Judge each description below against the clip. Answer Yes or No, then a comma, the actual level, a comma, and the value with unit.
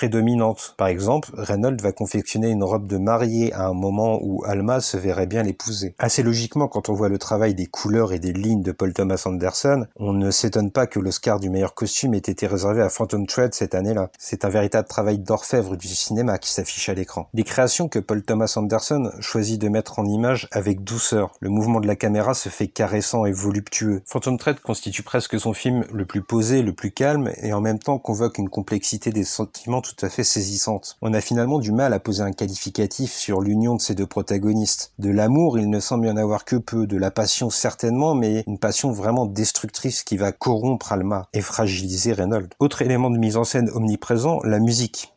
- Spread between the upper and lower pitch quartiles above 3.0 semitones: No, narrow, 2.6 semitones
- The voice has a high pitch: No, low, 110 Hz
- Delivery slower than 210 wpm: No, average, 215 wpm